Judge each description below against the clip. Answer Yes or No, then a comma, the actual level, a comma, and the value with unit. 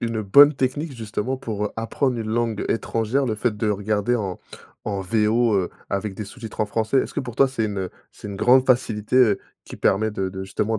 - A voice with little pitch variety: No, average, 3.0 semitones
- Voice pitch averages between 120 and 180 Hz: No, low, 110 Hz